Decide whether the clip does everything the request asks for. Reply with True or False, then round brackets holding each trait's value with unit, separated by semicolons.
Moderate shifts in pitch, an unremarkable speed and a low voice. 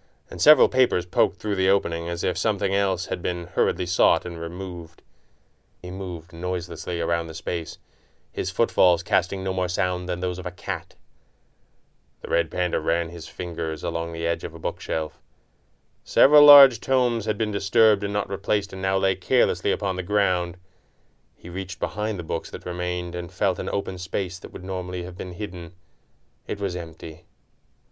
False (2.3 semitones; 180 wpm; 90 Hz)